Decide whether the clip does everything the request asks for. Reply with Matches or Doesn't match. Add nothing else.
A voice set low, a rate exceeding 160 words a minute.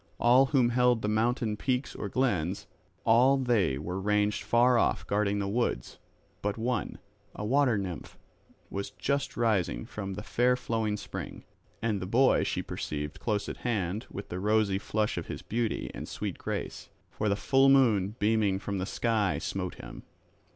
Matches